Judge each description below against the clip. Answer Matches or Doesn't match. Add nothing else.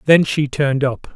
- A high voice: Doesn't match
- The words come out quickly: Matches